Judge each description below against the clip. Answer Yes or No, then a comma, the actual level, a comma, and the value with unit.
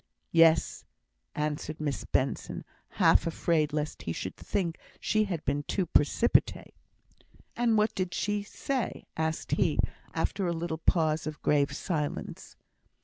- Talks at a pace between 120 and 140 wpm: Yes, slow, 135 wpm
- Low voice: No, medium, 160 Hz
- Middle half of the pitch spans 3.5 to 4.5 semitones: Yes, average, 3.8 semitones